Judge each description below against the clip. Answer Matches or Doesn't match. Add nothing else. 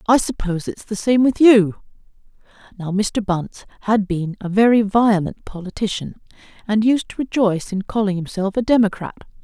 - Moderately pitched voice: Doesn't match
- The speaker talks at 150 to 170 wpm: Matches